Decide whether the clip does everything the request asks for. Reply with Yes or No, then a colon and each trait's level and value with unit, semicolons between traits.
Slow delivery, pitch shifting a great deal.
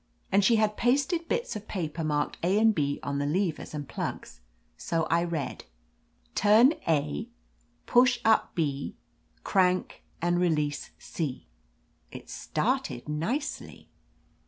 Yes: slow, 130 wpm; wide, 6.5 semitones